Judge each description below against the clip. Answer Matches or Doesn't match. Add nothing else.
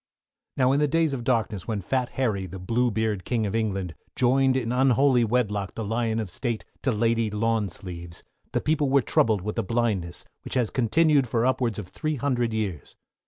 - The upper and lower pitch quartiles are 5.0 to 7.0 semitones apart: Doesn't match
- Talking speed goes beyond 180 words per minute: Matches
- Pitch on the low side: Matches